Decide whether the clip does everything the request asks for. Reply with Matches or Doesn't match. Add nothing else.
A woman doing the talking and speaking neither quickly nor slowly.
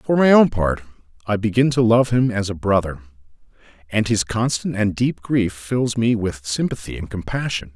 Doesn't match